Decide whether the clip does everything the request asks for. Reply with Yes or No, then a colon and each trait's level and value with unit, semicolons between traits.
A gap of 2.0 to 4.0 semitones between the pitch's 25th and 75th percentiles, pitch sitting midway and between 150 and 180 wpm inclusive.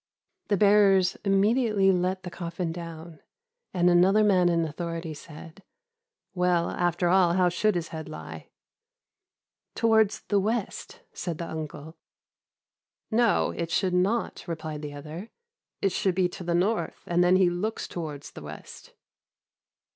No: average, 2.7 semitones; medium, 180 Hz; average, 140 wpm